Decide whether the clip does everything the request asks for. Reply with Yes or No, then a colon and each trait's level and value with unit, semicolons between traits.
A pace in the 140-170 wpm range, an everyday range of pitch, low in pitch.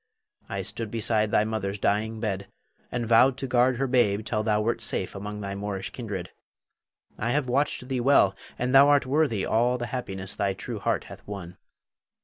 No: average, 185 wpm; average, 3.7 semitones; low, 110 Hz